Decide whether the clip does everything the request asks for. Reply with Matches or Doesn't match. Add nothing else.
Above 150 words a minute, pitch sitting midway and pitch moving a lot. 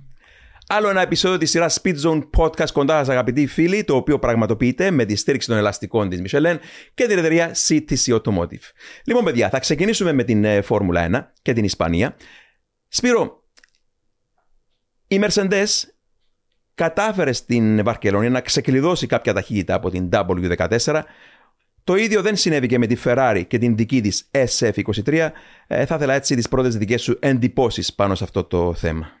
Doesn't match